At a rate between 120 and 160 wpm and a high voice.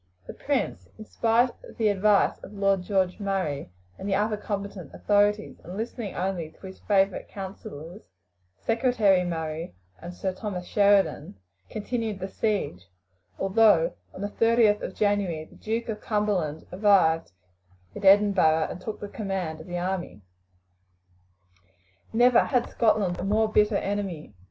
Yes: average, 145 wpm; high, 195 Hz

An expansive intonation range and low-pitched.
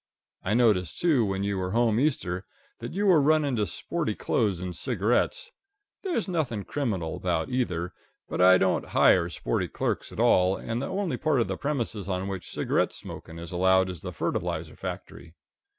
Yes: wide, 7.0 semitones; low, 100 Hz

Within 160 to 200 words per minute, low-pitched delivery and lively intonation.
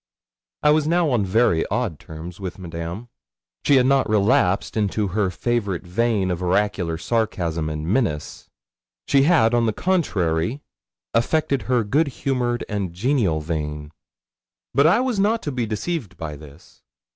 No: average, 150 wpm; low, 105 Hz; wide, 7.3 semitones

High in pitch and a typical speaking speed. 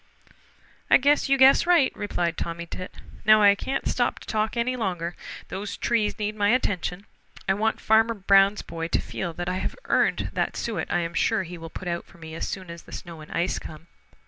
No: high, 195 Hz; fast, 215 wpm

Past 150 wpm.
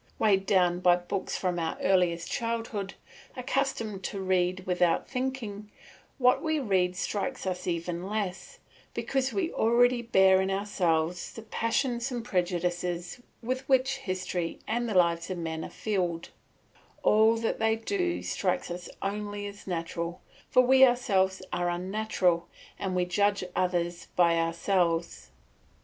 No: average, 140 wpm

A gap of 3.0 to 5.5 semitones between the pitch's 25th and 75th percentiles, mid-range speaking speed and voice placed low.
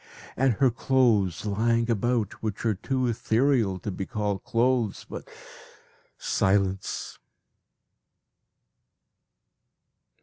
No: average, 3.6 semitones; slow, 90 wpm; low, 115 Hz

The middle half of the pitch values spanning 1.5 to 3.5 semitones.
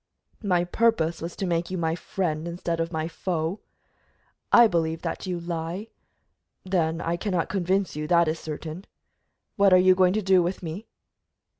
Yes: narrow, 2.4 semitones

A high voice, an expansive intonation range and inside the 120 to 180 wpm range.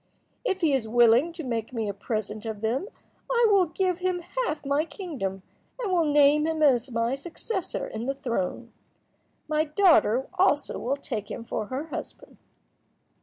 Yes: very high, 280 Hz; wide, 6.6 semitones; average, 170 wpm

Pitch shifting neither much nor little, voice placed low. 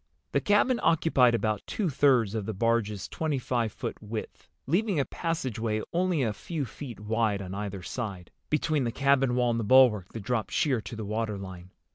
Yes: average, 4.8 semitones; low, 115 Hz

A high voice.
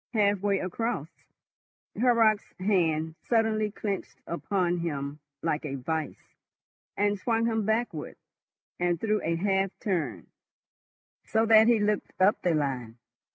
Yes: high, 195 Hz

